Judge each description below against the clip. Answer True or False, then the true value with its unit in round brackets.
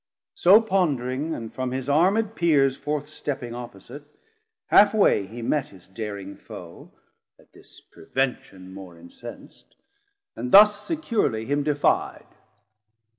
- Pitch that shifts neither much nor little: False (7.0 semitones)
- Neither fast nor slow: False (125 wpm)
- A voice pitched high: False (135 Hz)